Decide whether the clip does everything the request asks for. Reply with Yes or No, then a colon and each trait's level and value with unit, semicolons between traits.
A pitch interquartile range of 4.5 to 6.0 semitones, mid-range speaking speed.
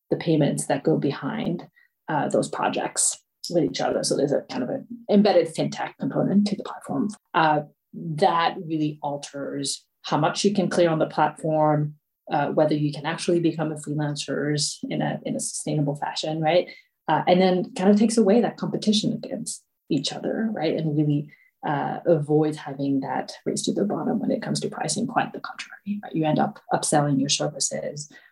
Yes: average, 5.3 semitones; average, 185 wpm